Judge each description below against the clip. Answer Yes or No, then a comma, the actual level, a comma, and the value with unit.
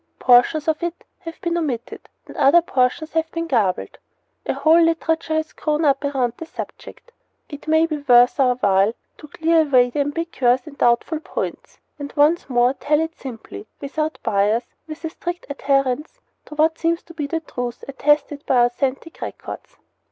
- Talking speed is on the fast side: No, average, 190 wpm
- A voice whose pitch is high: Yes, very high, 295 Hz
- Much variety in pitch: No, average, 4.4 semitones